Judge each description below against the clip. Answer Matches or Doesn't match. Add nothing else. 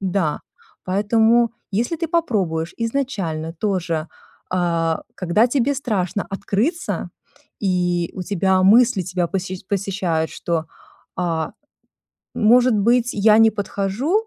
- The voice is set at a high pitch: Matches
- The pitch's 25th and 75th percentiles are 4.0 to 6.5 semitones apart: Matches